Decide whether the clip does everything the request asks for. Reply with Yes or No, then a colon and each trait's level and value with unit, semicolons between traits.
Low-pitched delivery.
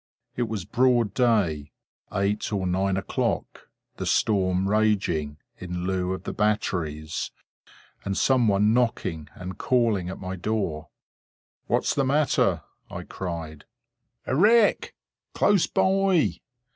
Yes: low, 100 Hz